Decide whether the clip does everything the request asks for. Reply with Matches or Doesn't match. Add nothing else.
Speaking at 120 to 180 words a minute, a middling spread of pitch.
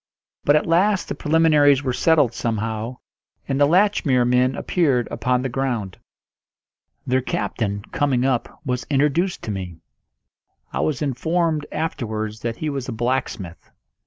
Matches